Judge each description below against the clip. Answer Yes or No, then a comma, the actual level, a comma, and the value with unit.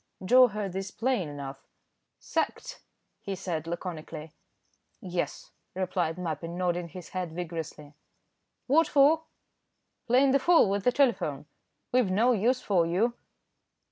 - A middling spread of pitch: No, wide, 6.8 semitones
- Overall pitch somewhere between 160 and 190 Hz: Yes, medium, 185 Hz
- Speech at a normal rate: No, slow, 125 wpm